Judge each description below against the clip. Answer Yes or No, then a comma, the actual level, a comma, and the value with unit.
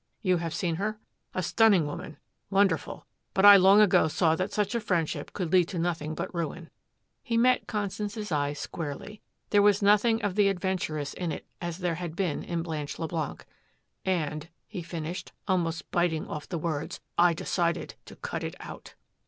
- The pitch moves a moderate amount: Yes, average, 3.8 semitones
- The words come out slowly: No, average, 175 wpm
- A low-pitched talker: No, medium, 175 Hz